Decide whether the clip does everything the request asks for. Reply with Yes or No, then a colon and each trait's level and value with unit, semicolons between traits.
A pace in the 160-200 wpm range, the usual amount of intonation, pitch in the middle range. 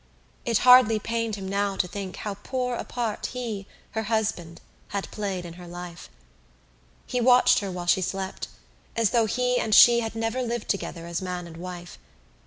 No: average, 185 wpm; average, 4.3 semitones; high, 205 Hz